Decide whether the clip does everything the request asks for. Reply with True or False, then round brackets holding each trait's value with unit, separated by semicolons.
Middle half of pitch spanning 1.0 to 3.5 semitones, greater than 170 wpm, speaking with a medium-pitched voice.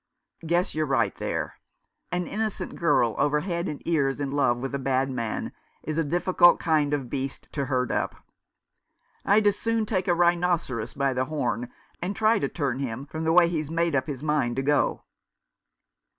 False (4.4 semitones; 190 wpm; 150 Hz)